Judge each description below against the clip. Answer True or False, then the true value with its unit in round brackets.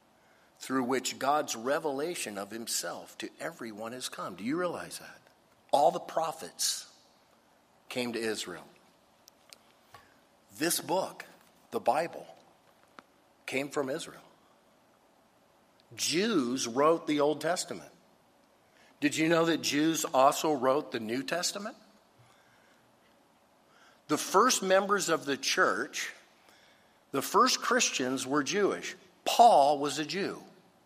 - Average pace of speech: False (110 wpm)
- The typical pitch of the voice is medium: True (145 Hz)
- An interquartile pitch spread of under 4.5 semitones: False (4.8 semitones)